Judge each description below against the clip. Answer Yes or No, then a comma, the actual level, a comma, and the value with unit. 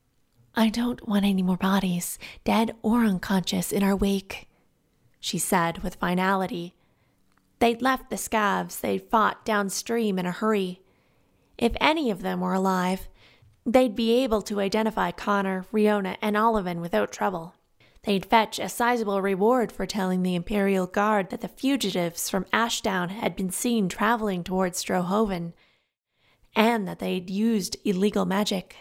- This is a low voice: No, high, 200 Hz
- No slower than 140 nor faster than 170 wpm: Yes, average, 145 wpm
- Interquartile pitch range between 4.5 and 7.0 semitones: No, average, 3.1 semitones